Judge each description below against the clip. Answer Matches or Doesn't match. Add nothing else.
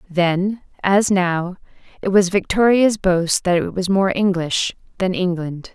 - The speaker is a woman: Matches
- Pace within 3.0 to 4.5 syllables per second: Matches